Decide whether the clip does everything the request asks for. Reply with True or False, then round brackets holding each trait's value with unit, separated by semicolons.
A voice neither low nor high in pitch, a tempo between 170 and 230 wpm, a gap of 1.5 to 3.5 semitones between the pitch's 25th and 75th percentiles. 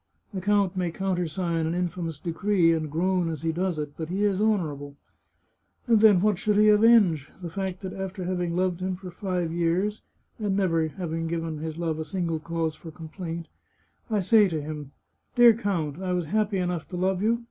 True (180 Hz; 195 wpm; 2.9 semitones)